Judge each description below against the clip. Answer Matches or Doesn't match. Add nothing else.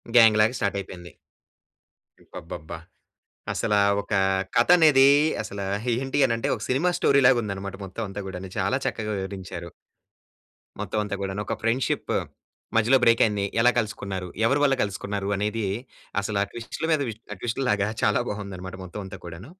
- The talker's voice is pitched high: Doesn't match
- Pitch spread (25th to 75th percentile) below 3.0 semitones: Doesn't match